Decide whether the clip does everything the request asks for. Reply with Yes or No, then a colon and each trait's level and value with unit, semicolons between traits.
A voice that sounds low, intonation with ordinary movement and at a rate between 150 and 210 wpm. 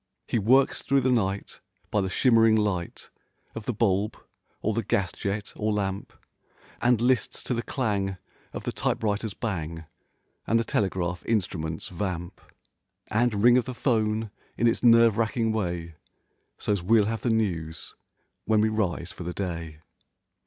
Yes: low, 105 Hz; average, 3.6 semitones; average, 155 wpm